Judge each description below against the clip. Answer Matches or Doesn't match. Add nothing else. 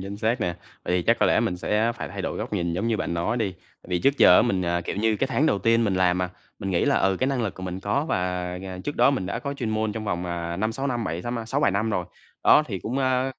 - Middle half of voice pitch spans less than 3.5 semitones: Doesn't match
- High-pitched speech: Doesn't match